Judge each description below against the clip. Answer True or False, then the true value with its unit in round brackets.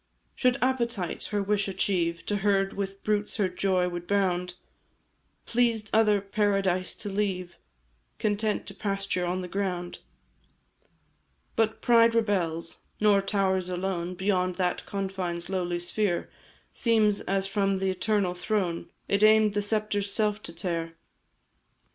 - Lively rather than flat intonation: False (2.5 semitones)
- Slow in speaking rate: True (130 wpm)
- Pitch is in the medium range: False (195 Hz)